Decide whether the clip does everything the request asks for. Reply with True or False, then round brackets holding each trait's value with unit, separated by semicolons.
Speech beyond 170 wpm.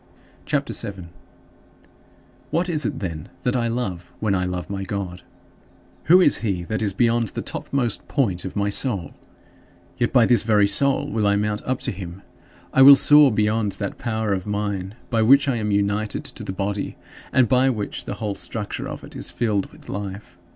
True (195 wpm)